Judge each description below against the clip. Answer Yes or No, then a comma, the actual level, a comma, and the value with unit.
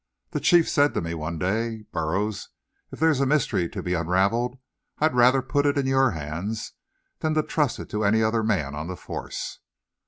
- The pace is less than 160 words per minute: No, average, 195 wpm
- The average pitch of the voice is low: Yes, low, 110 Hz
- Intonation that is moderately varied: No, wide, 7.2 semitones